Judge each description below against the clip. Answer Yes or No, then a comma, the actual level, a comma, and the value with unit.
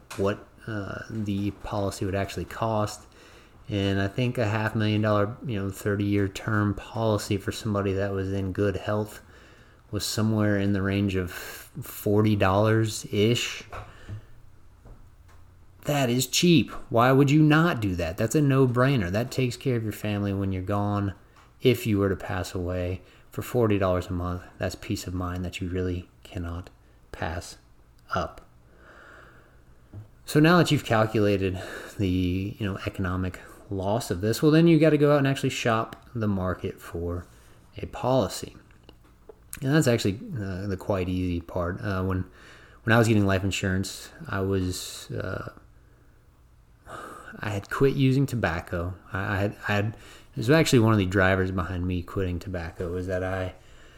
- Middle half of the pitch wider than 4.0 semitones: No, average, 3.2 semitones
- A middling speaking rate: Yes, average, 165 wpm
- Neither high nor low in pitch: No, low, 100 Hz